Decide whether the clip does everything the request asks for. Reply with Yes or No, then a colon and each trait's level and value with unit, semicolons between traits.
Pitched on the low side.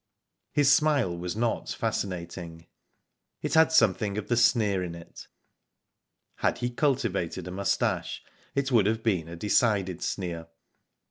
Yes: low, 100 Hz